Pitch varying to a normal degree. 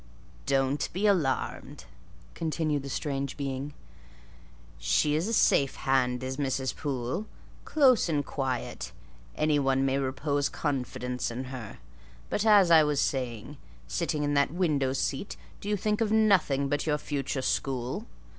Yes: average, 3.2 semitones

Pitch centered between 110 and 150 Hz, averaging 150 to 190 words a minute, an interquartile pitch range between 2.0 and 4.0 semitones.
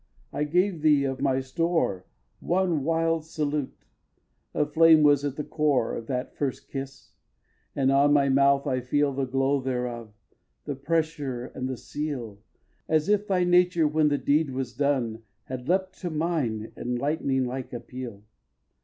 Yes: medium, 140 Hz; average, 160 wpm; average, 3.3 semitones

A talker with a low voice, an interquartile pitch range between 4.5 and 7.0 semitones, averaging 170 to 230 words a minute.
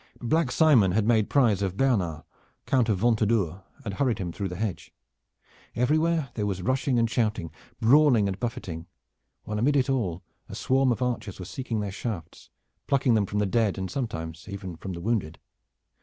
Yes: low, 110 Hz; average, 4.8 semitones; average, 180 wpm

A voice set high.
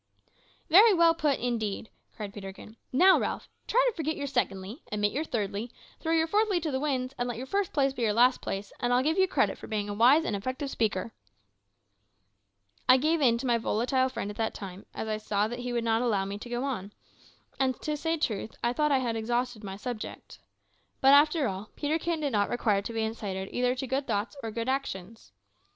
Yes: high, 245 Hz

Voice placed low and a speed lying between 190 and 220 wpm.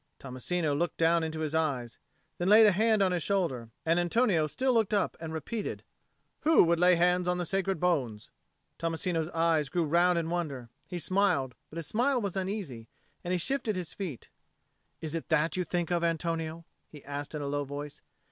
No: medium, 170 Hz; average, 195 wpm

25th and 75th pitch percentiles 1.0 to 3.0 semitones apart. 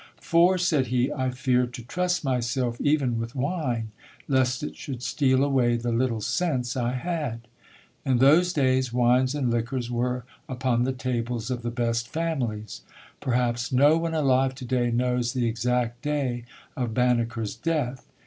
Yes: narrow, 2.4 semitones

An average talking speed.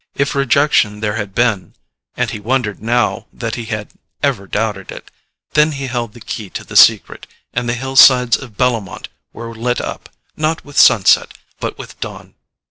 Yes: average, 165 wpm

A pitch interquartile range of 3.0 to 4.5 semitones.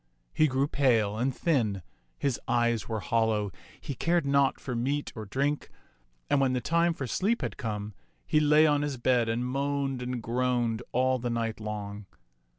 Yes: average, 3.8 semitones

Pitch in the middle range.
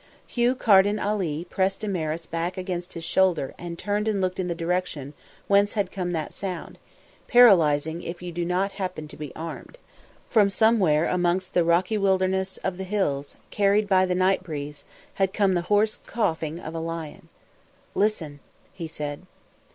Yes: medium, 180 Hz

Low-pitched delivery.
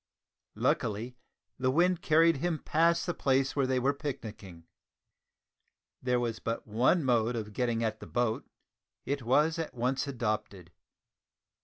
Yes: low, 125 Hz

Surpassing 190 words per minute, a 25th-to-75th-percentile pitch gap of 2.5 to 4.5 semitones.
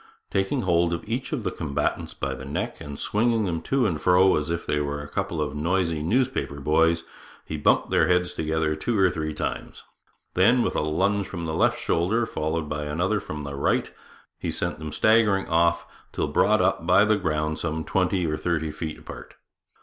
Yes: average, 200 wpm; average, 3.9 semitones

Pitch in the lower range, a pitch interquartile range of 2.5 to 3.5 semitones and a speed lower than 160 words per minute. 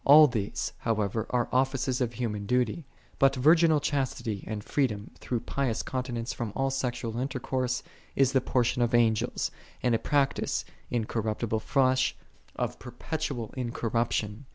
Yes: low, 125 Hz; average, 2.8 semitones; average, 140 wpm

